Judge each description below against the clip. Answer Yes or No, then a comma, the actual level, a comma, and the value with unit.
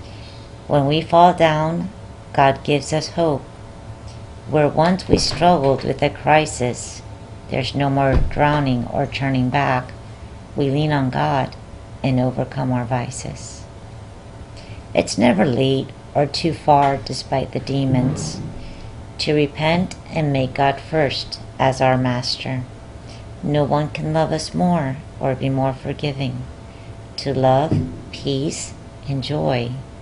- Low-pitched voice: Yes, low, 130 Hz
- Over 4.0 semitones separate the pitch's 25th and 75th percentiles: Yes, average, 4.6 semitones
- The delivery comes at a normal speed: No, slow, 125 wpm